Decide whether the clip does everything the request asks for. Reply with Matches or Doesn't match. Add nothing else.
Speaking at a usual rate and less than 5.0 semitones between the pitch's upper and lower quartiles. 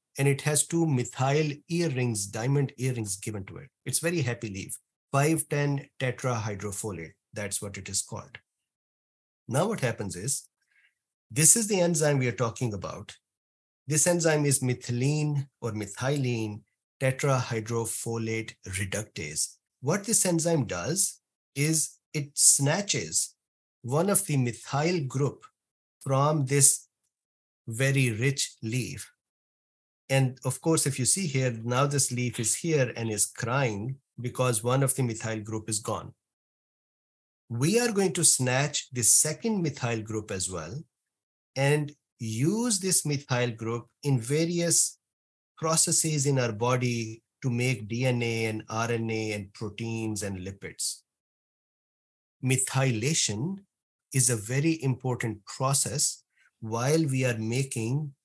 Doesn't match